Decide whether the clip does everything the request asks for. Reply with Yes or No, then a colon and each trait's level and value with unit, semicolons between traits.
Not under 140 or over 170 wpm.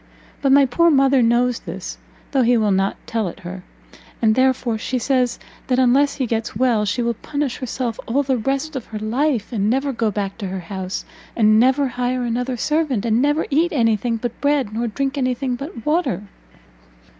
No: average, 200 wpm